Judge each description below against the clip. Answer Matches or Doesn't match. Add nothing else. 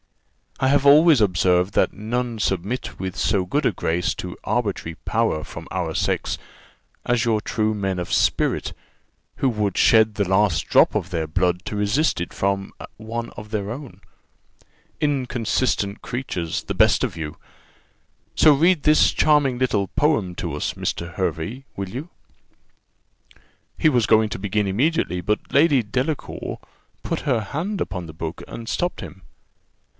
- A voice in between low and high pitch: Doesn't match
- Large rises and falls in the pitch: Matches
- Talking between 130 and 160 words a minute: Matches